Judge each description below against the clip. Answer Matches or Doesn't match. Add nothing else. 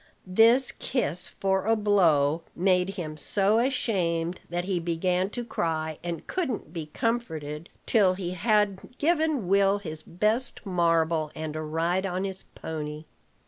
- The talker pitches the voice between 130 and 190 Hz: Matches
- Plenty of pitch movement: Doesn't match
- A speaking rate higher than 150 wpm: Doesn't match